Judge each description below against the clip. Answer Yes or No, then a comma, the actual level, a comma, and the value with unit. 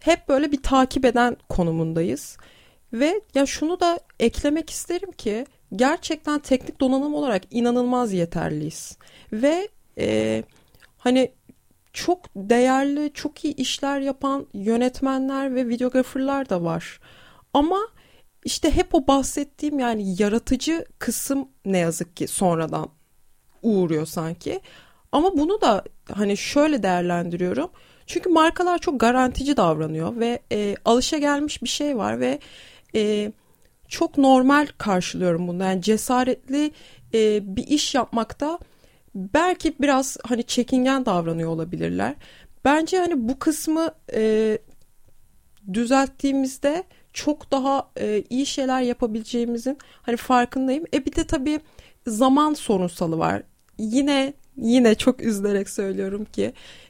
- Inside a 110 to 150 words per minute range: Yes, average, 115 wpm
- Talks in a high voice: Yes, very high, 260 Hz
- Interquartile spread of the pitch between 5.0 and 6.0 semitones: Yes, average, 5.3 semitones